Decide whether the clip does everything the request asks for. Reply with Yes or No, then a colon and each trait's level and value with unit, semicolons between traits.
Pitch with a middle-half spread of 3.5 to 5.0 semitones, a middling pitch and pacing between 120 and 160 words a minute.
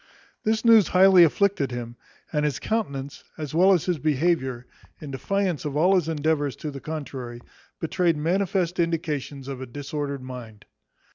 Yes: average, 4.7 semitones; medium, 150 Hz; average, 155 wpm